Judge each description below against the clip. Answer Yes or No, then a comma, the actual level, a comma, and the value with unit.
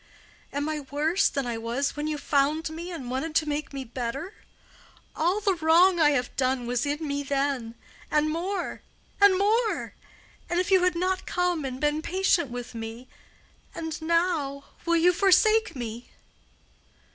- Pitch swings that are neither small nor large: Yes, average, 4.6 semitones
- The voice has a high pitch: Yes, very high, 305 Hz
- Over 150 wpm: No, average, 145 wpm